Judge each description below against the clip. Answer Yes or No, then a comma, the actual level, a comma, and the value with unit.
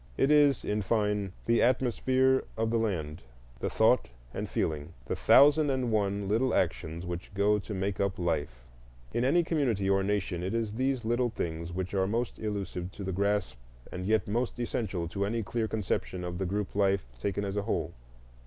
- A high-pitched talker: No, low, 100 Hz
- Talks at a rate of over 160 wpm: Yes, average, 190 wpm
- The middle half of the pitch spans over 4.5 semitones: No, average, 3.8 semitones